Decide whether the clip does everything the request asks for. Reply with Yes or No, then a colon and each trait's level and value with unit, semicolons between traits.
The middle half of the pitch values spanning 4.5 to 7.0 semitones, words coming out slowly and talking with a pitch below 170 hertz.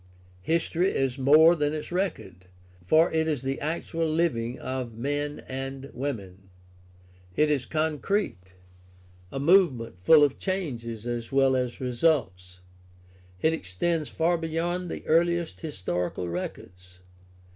Yes: wide, 5.6 semitones; slow, 125 wpm; medium, 140 Hz